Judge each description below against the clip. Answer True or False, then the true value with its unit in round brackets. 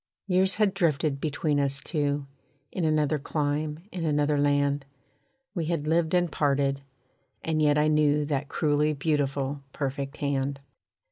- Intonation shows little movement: True (1.7 semitones)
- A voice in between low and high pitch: True (150 Hz)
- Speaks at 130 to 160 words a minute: True (140 wpm)